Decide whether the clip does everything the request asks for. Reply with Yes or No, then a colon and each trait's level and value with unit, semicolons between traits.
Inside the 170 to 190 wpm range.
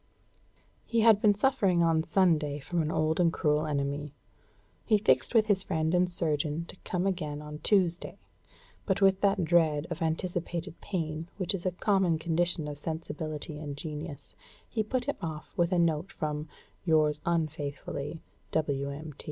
No: average, 160 wpm